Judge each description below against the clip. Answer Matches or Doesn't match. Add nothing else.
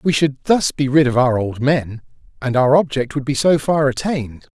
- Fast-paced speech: Matches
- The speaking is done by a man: Matches